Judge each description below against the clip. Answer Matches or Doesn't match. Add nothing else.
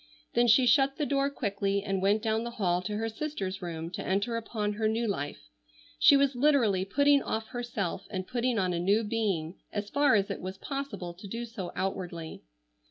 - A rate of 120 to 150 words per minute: Doesn't match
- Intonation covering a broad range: Doesn't match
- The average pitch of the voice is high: Matches